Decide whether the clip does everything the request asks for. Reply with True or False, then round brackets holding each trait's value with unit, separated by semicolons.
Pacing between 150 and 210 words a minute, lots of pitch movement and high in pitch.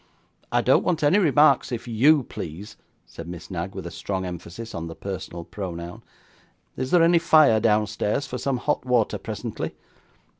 False (165 wpm; 7.9 semitones; 110 Hz)